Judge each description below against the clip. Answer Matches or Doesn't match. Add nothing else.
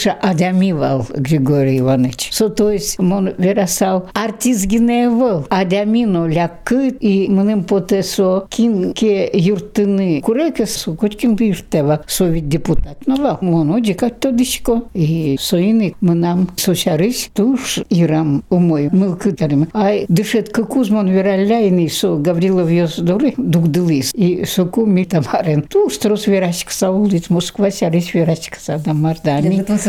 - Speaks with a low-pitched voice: Doesn't match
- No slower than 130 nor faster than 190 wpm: Doesn't match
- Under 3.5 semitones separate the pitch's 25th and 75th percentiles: Doesn't match